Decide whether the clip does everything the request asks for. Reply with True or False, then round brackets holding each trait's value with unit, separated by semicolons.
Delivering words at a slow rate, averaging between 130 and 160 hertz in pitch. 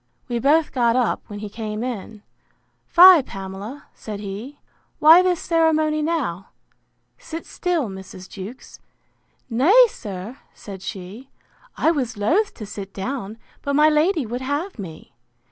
False (130 wpm; 250 Hz)